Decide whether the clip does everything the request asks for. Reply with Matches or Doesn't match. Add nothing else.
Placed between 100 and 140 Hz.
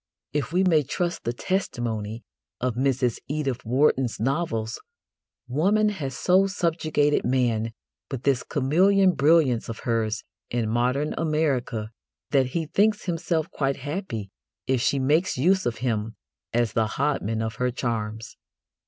Matches